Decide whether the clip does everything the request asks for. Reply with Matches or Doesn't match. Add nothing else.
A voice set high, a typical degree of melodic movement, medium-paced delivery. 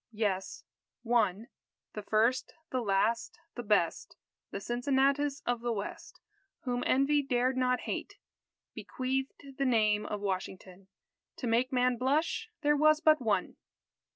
Doesn't match